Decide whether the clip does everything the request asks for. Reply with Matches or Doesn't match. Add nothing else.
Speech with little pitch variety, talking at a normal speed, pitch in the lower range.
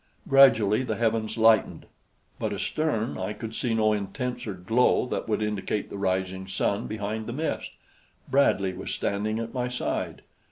Doesn't match